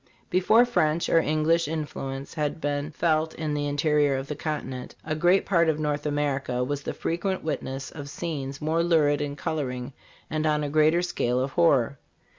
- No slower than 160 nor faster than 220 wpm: Yes, average, 180 wpm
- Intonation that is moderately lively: No, narrow, 2.3 semitones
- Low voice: No, medium, 150 Hz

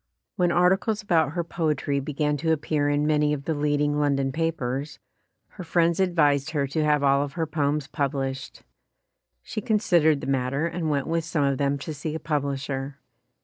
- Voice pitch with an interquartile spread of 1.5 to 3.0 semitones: Yes, average, 2.7 semitones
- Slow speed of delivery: No, average, 190 wpm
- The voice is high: No, medium, 150 Hz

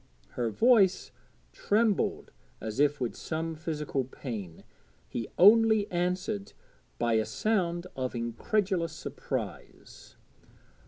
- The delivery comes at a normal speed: No, slow, 100 wpm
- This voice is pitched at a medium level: Yes, medium, 165 Hz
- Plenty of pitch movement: Yes, wide, 8.4 semitones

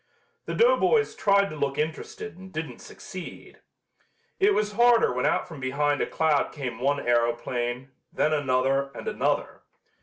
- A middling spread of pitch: No, wide, 6.6 semitones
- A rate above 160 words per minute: No, average, 150 wpm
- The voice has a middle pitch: Yes, medium, 145 Hz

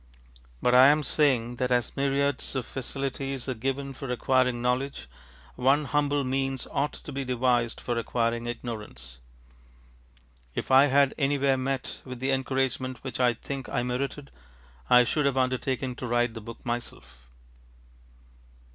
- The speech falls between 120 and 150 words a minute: Yes, average, 145 wpm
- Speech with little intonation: Yes, narrow, 2.0 semitones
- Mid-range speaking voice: No, low, 130 Hz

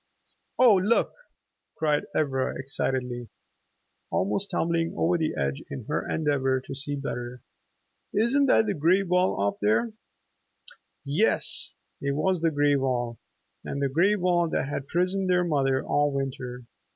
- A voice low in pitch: No, medium, 145 Hz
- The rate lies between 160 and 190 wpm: No, average, 140 wpm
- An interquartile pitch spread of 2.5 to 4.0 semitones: No, average, 5.3 semitones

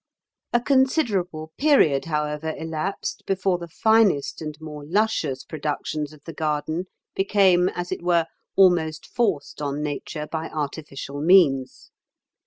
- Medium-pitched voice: Yes, medium, 160 Hz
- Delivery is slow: Yes, slow, 125 wpm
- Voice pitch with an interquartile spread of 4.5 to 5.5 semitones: No, average, 4.0 semitones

